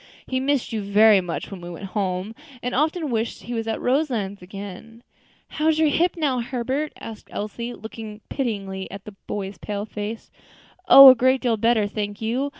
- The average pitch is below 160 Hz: No, high, 225 Hz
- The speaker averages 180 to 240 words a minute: Yes, average, 185 wpm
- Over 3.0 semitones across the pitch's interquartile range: Yes, average, 4.2 semitones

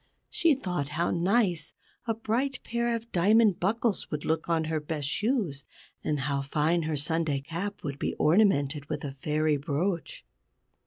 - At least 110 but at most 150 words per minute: No, average, 160 wpm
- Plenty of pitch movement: Yes, wide, 6.0 semitones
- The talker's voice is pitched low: No, medium, 165 Hz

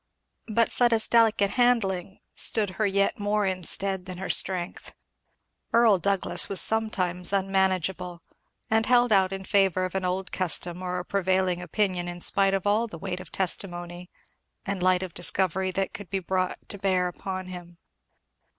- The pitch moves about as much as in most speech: No, narrow, 1.8 semitones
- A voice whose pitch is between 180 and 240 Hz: Yes, high, 190 Hz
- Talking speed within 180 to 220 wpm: No, average, 165 wpm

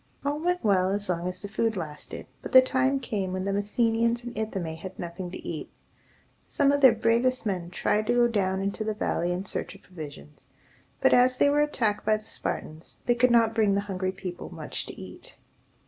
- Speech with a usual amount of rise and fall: Yes, average, 4.5 semitones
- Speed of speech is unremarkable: No, fast, 210 wpm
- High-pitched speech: Yes, high, 210 Hz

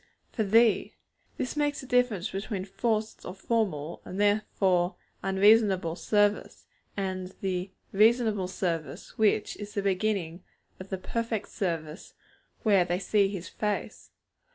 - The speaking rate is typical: No, slow, 130 wpm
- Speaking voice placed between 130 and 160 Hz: No, high, 200 Hz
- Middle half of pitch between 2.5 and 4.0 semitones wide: Yes, average, 2.9 semitones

